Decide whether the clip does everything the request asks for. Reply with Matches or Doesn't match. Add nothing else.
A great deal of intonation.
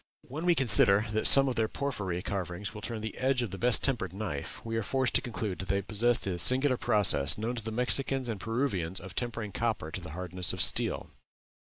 Doesn't match